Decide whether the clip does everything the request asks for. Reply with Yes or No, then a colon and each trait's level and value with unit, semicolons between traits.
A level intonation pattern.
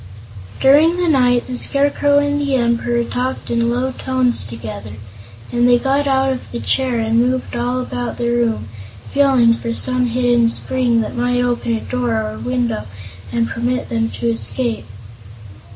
Yes: narrow, 2.0 semitones